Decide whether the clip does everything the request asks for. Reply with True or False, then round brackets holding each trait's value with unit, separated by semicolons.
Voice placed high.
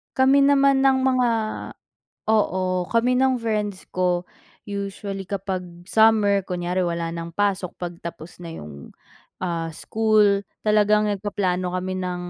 True (200 Hz)